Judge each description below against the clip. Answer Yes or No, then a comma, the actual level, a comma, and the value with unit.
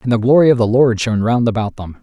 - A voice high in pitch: No, low, 115 Hz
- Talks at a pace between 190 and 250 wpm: No, fast, 295 wpm